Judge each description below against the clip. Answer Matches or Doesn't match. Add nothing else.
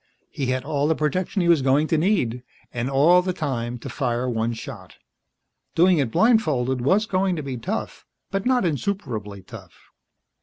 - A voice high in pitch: Doesn't match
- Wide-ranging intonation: Matches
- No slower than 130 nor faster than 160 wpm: Doesn't match